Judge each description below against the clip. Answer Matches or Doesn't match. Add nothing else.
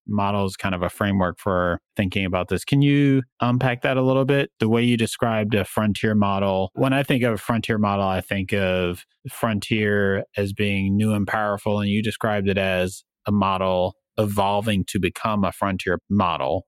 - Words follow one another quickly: Doesn't match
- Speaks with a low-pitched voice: Matches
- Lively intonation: Doesn't match